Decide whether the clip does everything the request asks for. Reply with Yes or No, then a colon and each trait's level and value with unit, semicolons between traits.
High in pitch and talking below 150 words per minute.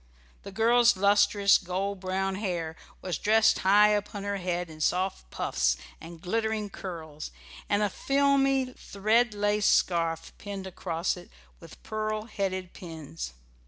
Yes: high, 195 Hz; slow, 135 wpm